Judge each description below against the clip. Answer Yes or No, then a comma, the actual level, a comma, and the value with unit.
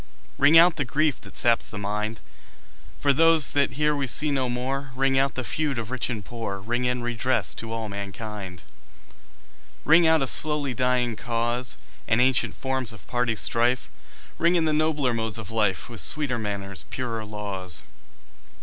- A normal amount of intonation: Yes, average, 4.0 semitones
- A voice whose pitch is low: Yes, low, 125 Hz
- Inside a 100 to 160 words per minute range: No, average, 175 wpm